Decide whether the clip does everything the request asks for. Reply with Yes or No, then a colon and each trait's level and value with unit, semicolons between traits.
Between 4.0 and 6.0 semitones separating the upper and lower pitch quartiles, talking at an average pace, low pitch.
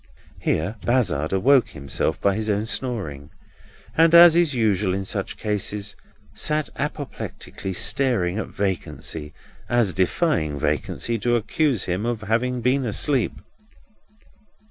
No: average, 5.1 semitones; slow, 120 wpm; low, 110 Hz